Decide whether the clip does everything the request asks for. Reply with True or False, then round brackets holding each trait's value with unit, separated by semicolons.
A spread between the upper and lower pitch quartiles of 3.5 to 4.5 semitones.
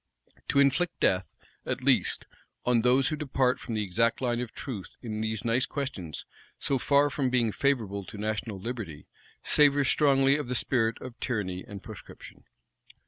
True (4.2 semitones)